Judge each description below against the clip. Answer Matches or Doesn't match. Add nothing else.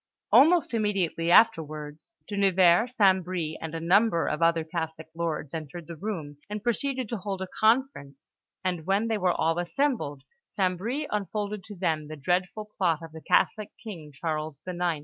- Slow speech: Doesn't match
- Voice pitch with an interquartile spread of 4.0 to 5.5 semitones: Matches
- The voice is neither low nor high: Matches